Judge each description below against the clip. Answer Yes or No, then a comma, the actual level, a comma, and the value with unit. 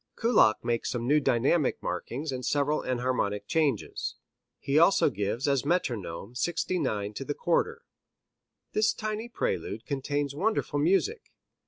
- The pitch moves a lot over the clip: Yes, wide, 6.6 semitones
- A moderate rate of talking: No, slow, 130 wpm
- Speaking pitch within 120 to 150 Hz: Yes, medium, 140 Hz